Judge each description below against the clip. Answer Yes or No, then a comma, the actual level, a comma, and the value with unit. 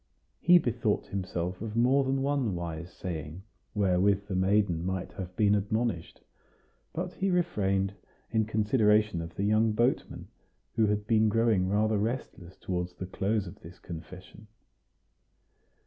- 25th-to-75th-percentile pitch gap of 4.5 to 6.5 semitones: No, average, 3.4 semitones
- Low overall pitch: Yes, low, 105 Hz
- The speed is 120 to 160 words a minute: Yes, average, 140 wpm